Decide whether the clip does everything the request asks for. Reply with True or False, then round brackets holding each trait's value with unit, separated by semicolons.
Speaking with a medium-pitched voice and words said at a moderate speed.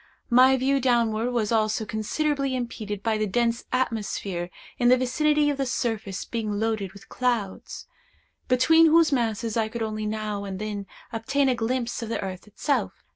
False (230 Hz; 170 wpm)